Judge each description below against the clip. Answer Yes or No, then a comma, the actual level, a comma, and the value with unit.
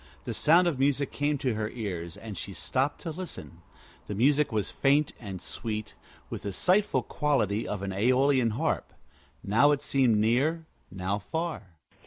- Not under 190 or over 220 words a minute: No, average, 165 wpm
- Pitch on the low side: Yes, low, 125 Hz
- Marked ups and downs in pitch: Yes, wide, 6.0 semitones